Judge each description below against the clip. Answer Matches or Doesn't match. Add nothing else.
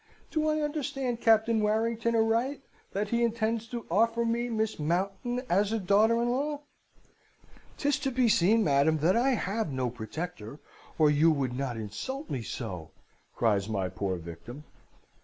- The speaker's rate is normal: Matches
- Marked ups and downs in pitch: Matches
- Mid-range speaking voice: Doesn't match